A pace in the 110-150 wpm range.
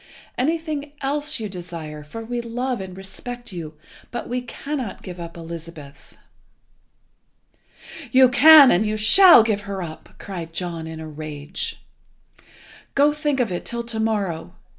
Yes: average, 145 wpm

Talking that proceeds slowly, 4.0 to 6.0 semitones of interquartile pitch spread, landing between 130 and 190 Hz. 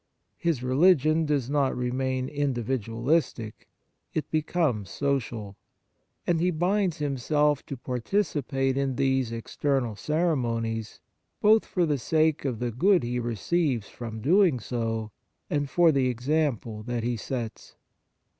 Yes: slow, 130 wpm; average, 4.7 semitones; low, 135 Hz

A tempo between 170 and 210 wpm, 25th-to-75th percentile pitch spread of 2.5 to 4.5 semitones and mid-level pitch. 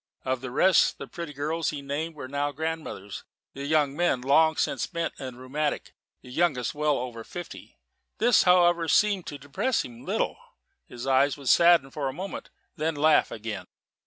Yes: average, 175 wpm; average, 3.9 semitones; medium, 145 Hz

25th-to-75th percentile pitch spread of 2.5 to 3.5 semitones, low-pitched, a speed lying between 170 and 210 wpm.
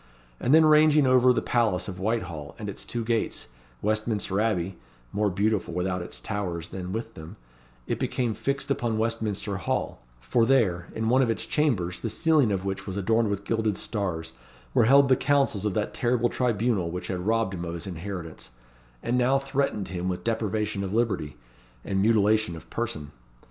No: average, 4.2 semitones; low, 105 Hz; average, 180 wpm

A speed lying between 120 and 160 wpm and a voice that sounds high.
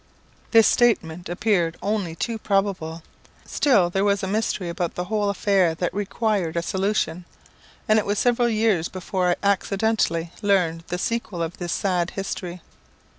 Yes: average, 155 wpm; high, 195 Hz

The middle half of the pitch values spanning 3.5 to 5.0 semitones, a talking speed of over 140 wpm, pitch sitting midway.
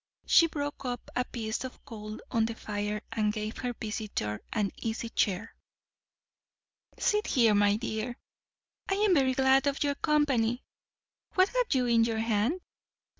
No: average, 4.2 semitones; average, 155 wpm; high, 235 Hz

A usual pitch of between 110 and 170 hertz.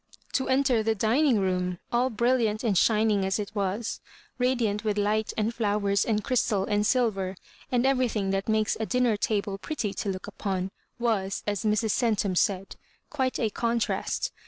No: high, 215 Hz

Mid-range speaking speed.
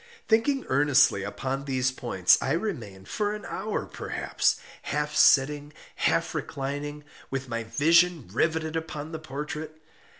No: slow, 130 wpm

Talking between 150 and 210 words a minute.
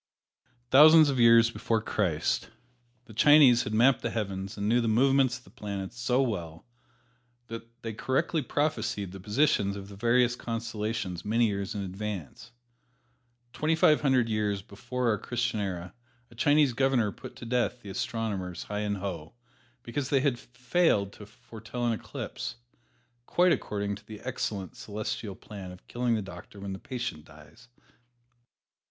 Yes: average, 160 wpm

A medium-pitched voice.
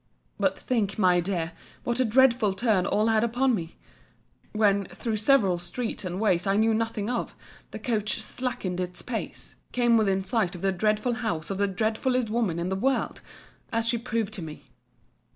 No: high, 215 Hz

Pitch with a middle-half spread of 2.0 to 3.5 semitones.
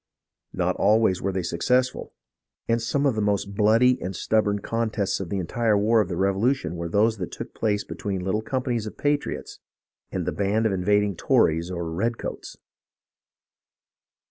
Yes: average, 3.2 semitones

